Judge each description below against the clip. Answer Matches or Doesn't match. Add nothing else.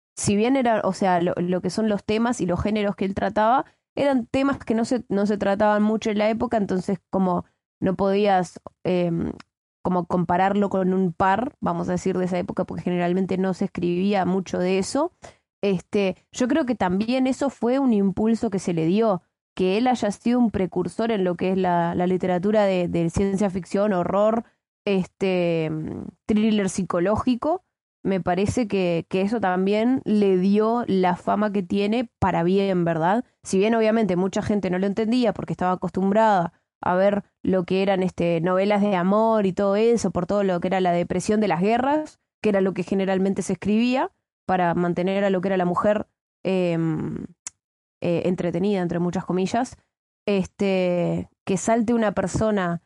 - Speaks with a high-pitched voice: Matches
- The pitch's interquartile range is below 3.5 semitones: Matches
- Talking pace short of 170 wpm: Doesn't match